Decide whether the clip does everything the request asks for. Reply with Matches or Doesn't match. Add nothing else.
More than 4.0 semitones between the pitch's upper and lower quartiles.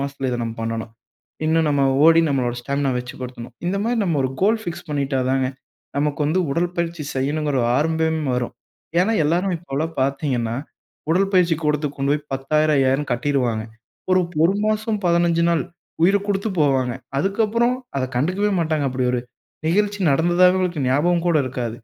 Matches